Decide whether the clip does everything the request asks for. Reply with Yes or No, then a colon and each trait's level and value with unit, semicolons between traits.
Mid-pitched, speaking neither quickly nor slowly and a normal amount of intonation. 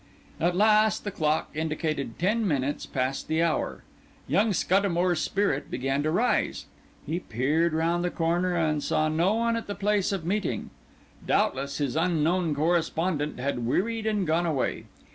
Yes: medium, 165 Hz; average, 155 wpm; average, 4.0 semitones